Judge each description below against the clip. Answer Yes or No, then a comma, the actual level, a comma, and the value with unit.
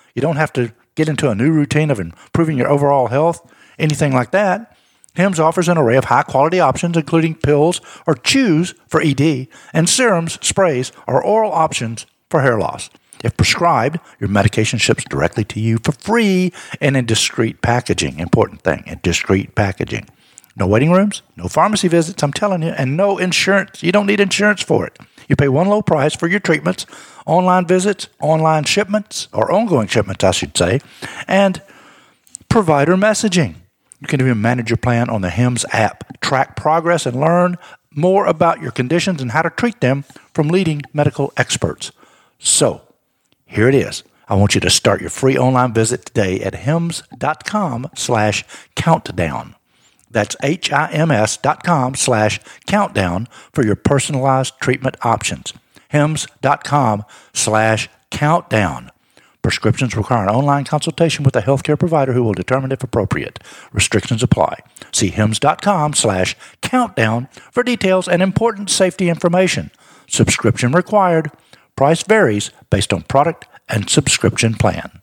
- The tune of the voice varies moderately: No, wide, 6.8 semitones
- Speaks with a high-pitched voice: No, medium, 145 Hz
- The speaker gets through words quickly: No, average, 150 wpm